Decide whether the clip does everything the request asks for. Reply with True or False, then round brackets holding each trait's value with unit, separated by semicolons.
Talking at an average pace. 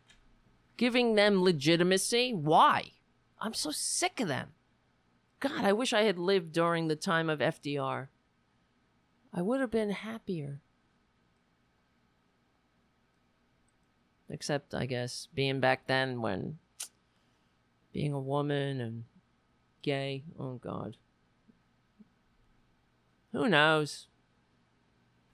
False (95 wpm)